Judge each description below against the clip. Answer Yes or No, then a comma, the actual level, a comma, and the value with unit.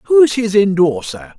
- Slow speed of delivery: Yes, slow, 130 wpm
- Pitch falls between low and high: Yes, medium, 155 Hz